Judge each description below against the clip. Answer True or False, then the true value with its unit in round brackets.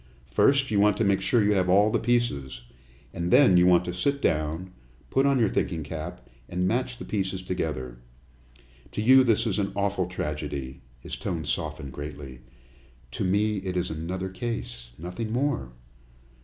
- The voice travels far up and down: True (5.8 semitones)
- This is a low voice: True (95 Hz)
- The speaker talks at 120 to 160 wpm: False (170 wpm)